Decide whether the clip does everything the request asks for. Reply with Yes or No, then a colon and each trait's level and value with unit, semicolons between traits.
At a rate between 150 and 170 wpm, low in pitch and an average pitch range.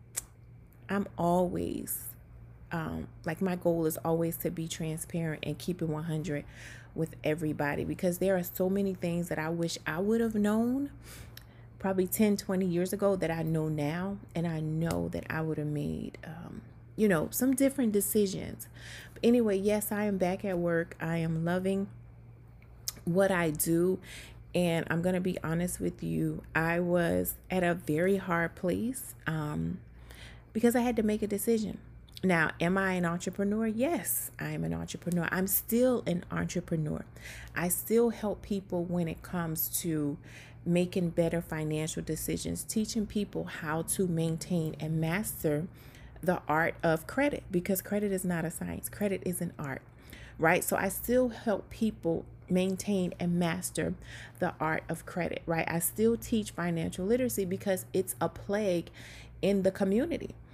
No: average, 160 wpm; medium, 170 Hz; average, 4.1 semitones